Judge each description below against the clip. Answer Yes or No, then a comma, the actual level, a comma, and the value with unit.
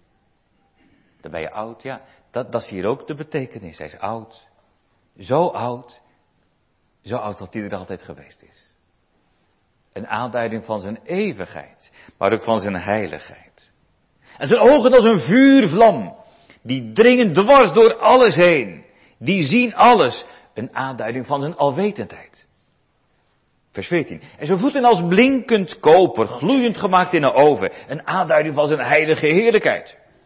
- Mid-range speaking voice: No, low, 130 Hz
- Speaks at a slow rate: No, average, 145 wpm